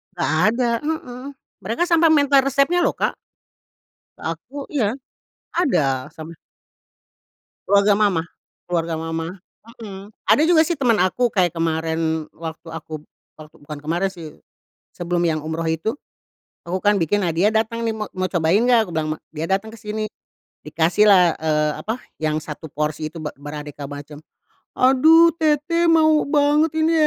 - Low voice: No, high, 190 Hz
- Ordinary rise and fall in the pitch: No, wide, 7.9 semitones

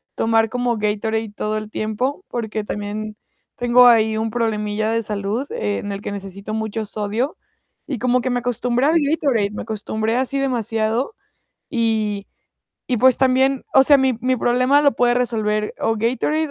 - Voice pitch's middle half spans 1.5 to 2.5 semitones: No, average, 2.9 semitones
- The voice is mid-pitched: No, high, 225 Hz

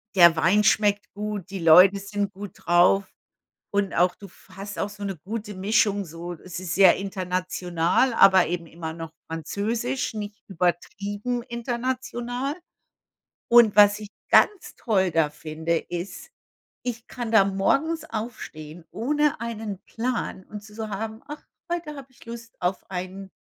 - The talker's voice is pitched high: Yes, high, 200 Hz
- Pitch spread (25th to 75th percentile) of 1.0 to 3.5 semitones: No, average, 4.2 semitones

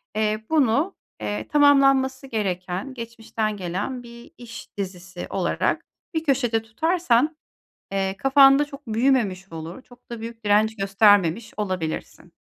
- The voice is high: Yes, high, 225 Hz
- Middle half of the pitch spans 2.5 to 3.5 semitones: No, average, 5.3 semitones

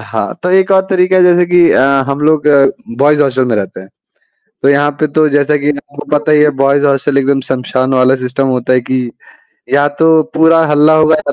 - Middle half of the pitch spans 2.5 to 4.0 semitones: Yes, average, 2.8 semitones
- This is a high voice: No, medium, 145 Hz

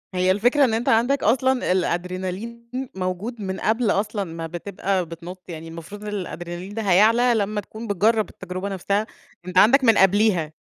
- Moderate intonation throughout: Yes, average, 3.5 semitones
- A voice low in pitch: No, high, 200 Hz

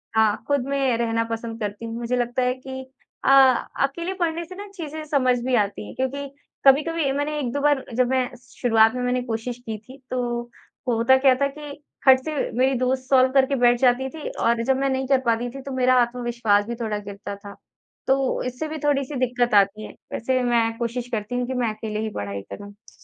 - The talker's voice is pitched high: Yes, very high, 250 Hz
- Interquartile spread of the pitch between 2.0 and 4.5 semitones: Yes, average, 2.9 semitones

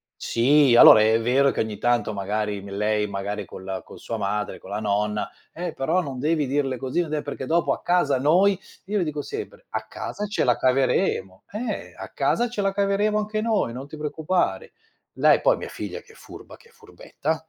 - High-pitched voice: No, medium, 140 Hz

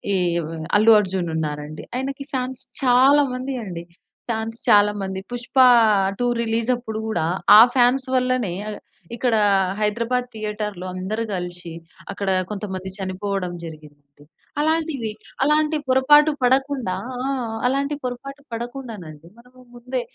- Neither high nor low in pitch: No, high, 225 Hz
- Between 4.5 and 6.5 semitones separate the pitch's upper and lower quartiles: Yes, average, 5.3 semitones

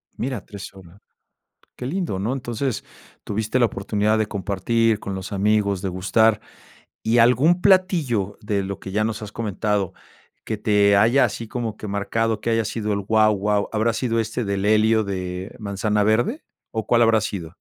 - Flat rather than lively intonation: Yes, narrow, 2.3 semitones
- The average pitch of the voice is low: Yes, low, 110 Hz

